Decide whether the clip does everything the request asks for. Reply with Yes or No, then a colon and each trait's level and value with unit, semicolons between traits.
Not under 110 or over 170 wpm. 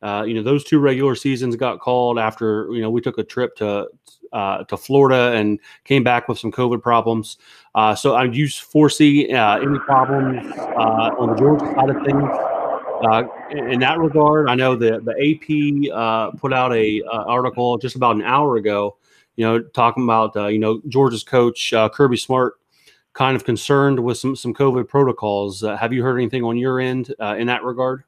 No: average, 200 wpm